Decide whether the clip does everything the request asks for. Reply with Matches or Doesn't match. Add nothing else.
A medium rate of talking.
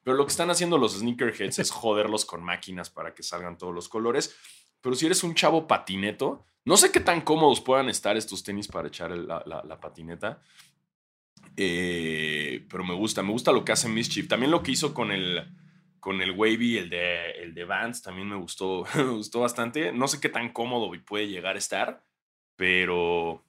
Doesn't match